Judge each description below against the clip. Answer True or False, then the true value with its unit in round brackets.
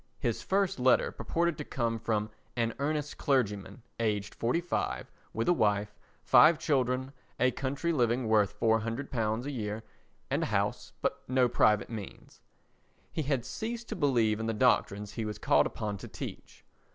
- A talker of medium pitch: False (120 Hz)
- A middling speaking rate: True (165 wpm)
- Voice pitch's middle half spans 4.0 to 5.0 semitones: True (4.5 semitones)